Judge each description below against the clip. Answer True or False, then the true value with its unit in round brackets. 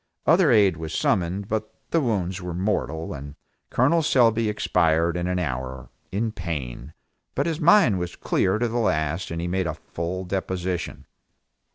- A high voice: False (95 Hz)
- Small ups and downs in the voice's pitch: False (4.9 semitones)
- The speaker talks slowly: False (165 wpm)